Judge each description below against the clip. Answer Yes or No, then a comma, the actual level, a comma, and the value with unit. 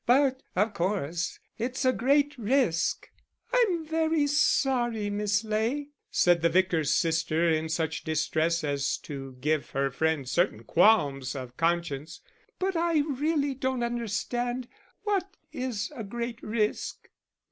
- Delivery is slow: Yes, slow, 130 wpm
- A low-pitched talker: No, high, 215 Hz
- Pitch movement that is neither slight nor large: No, wide, 8.4 semitones